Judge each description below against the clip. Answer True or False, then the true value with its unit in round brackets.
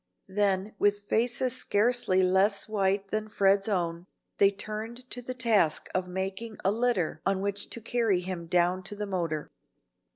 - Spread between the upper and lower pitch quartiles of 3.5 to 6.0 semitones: False (2.6 semitones)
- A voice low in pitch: False (200 Hz)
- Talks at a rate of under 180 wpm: True (160 wpm)